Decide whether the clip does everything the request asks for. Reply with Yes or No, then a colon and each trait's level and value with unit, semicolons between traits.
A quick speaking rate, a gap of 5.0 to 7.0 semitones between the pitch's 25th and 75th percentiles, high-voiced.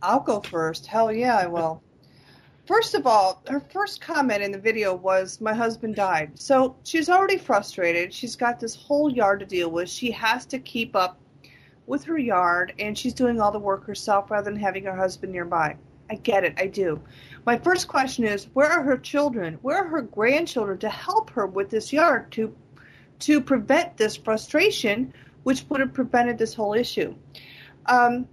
No: average, 190 wpm; wide, 5.6 semitones; high, 225 Hz